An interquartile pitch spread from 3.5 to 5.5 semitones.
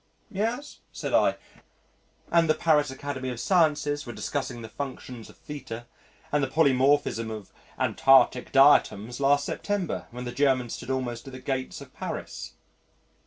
No: average, 3.0 semitones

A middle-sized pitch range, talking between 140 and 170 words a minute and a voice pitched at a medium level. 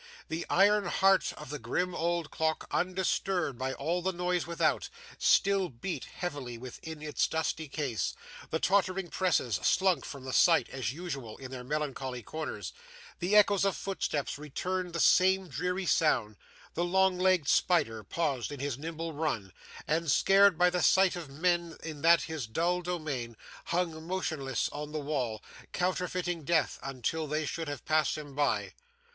Yes: average, 4.2 semitones; average, 160 wpm; medium, 160 Hz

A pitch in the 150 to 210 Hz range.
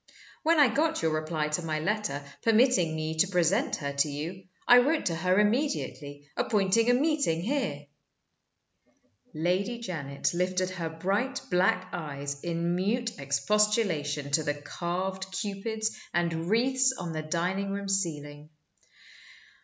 Yes: medium, 185 Hz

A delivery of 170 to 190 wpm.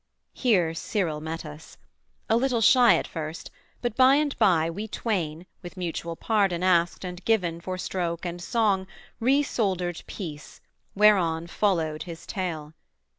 No: average, 140 wpm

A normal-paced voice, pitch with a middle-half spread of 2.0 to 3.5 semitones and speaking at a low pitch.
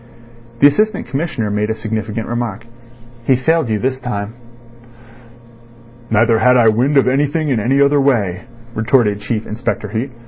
No: average, 150 wpm; average, 4.1 semitones; low, 120 Hz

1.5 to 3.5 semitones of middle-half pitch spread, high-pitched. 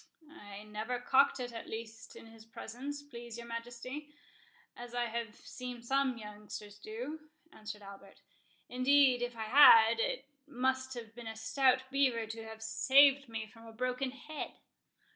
Yes: average, 2.9 semitones; high, 235 Hz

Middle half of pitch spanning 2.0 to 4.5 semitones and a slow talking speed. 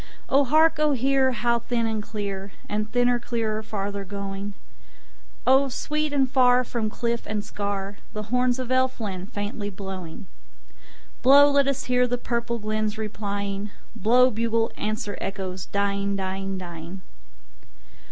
Yes: average, 3.8 semitones; slow, 125 wpm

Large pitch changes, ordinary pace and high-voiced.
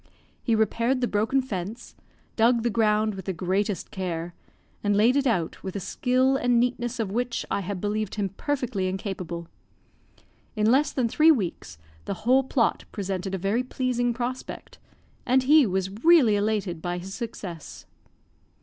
No: average, 4.4 semitones; average, 160 wpm; high, 215 Hz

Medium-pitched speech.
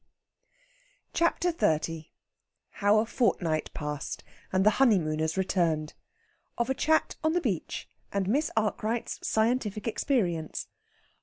No: high, 210 Hz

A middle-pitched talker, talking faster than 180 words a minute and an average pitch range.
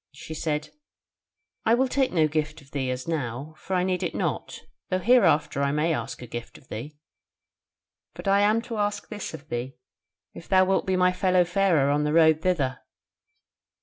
Yes: medium, 160 Hz; average, 190 wpm; average, 4.8 semitones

